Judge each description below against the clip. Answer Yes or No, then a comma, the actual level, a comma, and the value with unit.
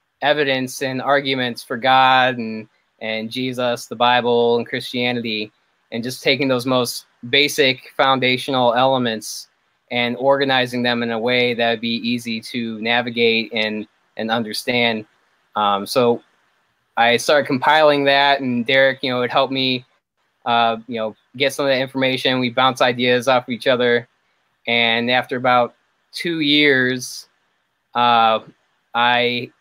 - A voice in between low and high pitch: No, low, 125 Hz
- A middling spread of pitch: No, narrow, 1.9 semitones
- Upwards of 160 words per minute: No, average, 140 wpm